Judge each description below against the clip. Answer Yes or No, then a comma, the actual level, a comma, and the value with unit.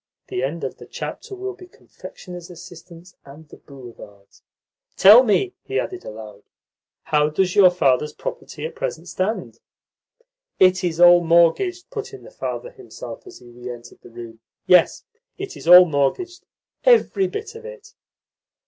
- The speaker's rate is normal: Yes, average, 155 wpm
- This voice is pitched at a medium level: Yes, medium, 180 Hz